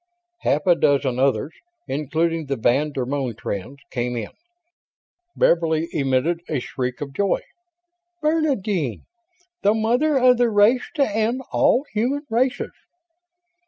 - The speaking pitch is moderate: Yes, medium, 165 Hz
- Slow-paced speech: Yes, slow, 125 wpm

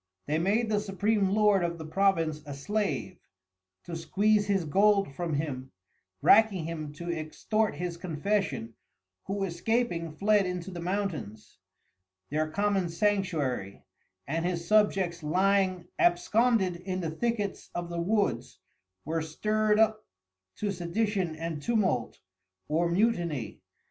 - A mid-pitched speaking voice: Yes, medium, 180 Hz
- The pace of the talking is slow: Yes, slow, 130 wpm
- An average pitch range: Yes, average, 4.2 semitones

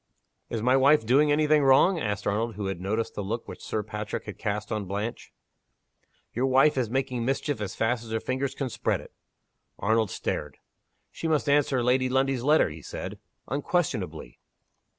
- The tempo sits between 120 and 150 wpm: No, average, 180 wpm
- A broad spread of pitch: No, average, 4.4 semitones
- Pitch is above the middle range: No, low, 120 Hz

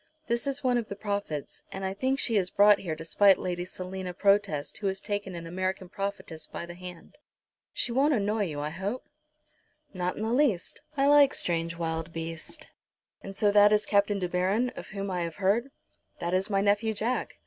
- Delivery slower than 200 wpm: No, fast, 205 wpm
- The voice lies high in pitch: Yes, high, 195 Hz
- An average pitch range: Yes, average, 3.2 semitones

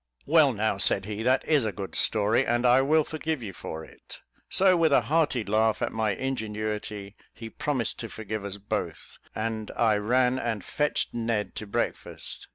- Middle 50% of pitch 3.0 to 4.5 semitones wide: Yes, average, 3.8 semitones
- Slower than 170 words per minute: No, average, 180 wpm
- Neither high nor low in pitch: No, low, 110 Hz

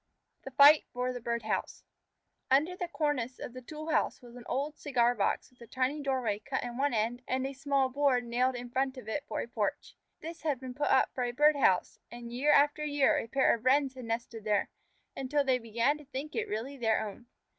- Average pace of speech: No, fast, 230 wpm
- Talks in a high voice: Yes, very high, 255 Hz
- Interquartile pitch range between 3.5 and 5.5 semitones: No, average, 3.1 semitones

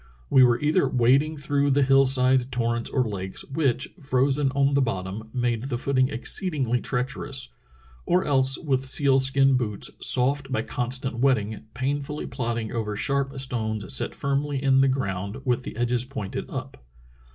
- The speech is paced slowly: No, average, 165 wpm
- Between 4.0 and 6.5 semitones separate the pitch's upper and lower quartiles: No, narrow, 2.5 semitones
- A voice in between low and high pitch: No, low, 130 Hz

